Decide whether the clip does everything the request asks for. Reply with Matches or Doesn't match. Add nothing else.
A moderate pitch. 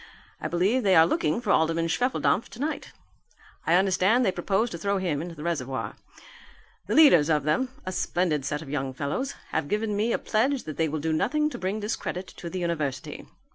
Matches